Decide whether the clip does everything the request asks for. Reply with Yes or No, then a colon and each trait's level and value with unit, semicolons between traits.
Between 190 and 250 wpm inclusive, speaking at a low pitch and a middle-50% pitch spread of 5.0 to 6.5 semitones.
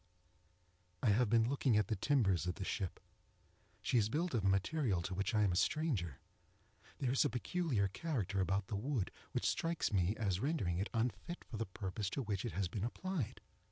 Yes: average, 200 wpm; low, 105 Hz; average, 5.3 semitones